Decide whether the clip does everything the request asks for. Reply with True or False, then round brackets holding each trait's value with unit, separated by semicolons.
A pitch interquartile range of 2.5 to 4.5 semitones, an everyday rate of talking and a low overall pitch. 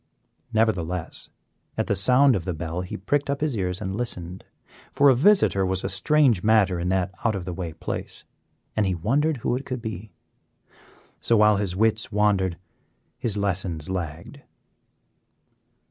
True (4.2 semitones; 160 wpm; 100 Hz)